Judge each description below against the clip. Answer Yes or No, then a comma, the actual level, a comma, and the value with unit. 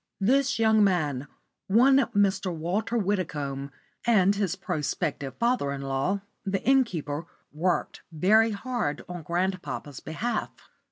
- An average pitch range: No, wide, 6.4 semitones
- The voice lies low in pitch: No, medium, 185 Hz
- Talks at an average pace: No, slow, 115 wpm